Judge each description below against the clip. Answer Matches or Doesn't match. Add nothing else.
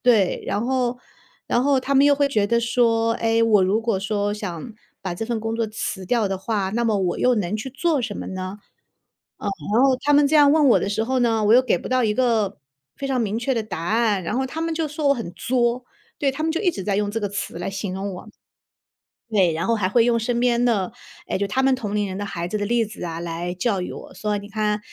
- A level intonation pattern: Doesn't match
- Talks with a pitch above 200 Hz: Matches